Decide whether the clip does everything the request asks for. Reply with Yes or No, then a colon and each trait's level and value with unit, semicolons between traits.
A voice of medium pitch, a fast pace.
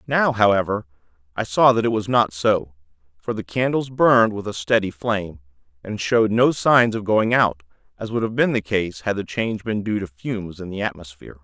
No: low, 105 Hz; fast, 210 wpm